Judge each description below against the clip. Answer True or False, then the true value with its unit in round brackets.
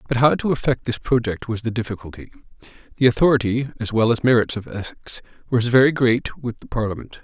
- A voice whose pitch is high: False (120 Hz)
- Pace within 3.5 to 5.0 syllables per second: False (6.0 syllables/s)